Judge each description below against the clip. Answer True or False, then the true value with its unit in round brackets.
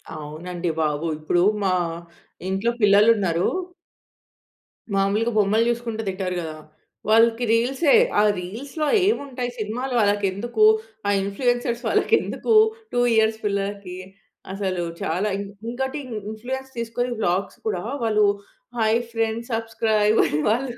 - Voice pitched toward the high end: True (220 Hz)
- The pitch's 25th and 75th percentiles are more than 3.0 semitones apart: True (3.5 semitones)